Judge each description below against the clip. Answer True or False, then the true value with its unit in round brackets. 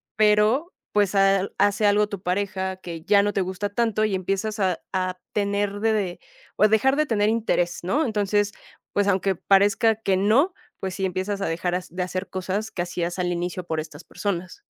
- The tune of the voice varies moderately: False (2.3 semitones)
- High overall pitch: True (195 Hz)